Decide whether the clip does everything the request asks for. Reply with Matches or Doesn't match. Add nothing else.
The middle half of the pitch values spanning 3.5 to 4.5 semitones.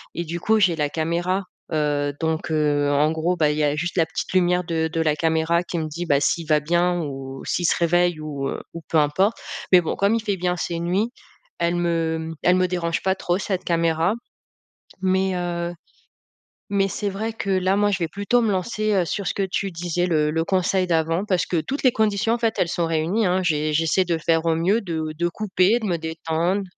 Doesn't match